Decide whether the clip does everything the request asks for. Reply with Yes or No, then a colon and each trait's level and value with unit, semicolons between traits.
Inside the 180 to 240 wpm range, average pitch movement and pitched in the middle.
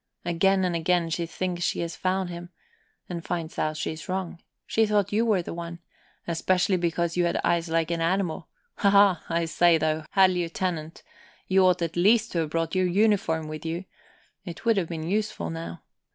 No: average, 185 wpm; narrow, 2.3 semitones; medium, 175 Hz